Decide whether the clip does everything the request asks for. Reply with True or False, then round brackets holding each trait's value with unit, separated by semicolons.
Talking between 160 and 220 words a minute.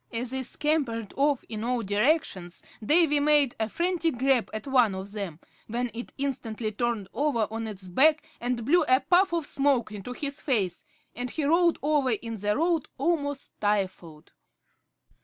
True (165 wpm)